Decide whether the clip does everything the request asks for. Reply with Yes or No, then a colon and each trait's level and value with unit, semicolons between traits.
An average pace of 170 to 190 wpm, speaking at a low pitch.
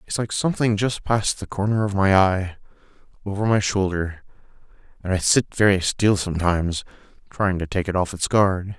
Yes: average, 180 wpm; low, 100 Hz